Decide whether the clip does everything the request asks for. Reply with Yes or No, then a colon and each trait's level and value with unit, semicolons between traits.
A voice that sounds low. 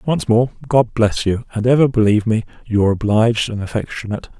Yes: low, 110 Hz